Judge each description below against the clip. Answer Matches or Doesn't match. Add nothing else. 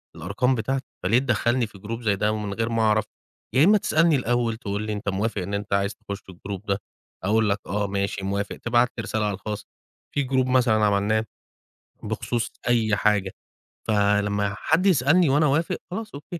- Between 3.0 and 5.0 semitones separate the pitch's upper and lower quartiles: Matches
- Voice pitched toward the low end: Matches